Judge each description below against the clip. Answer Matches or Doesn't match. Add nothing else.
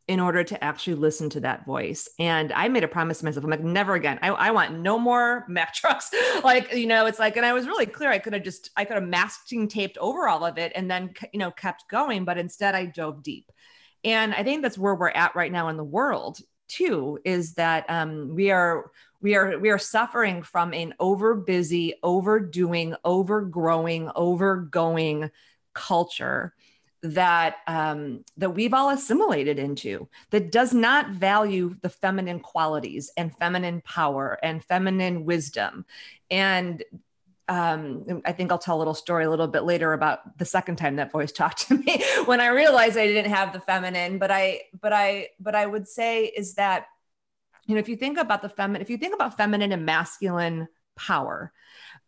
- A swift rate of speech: Doesn't match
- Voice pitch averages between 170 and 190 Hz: Matches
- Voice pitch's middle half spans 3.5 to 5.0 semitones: Matches